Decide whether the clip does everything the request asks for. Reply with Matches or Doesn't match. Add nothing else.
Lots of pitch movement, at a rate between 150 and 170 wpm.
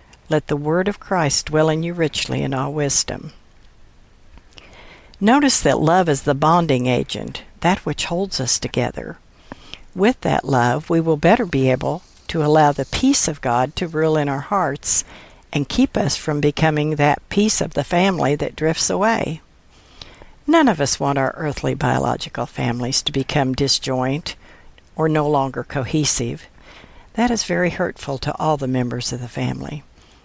Doesn't match